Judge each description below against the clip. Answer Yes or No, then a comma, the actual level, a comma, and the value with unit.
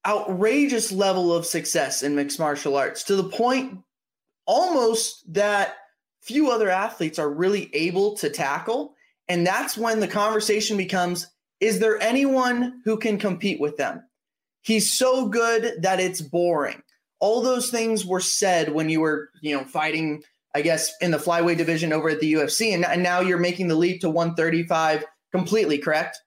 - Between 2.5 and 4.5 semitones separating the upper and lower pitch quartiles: No, average, 5.2 semitones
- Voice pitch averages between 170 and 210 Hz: Yes, medium, 185 Hz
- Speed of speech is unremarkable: Yes, average, 165 wpm